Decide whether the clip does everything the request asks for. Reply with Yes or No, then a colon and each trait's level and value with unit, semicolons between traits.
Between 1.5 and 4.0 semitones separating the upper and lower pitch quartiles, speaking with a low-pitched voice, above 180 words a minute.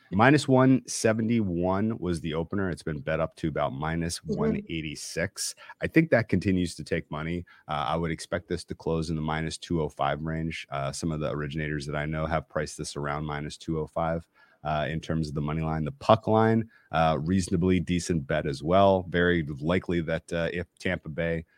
Yes: average, 3.4 semitones; very low, 85 Hz; average, 190 wpm